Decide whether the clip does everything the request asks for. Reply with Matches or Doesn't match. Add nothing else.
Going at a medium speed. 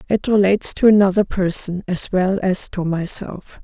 Matches